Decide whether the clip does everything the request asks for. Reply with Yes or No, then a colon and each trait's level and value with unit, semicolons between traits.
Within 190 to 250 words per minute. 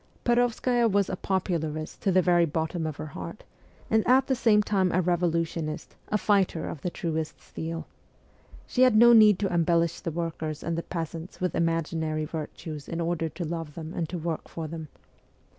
Yes: average, 195 wpm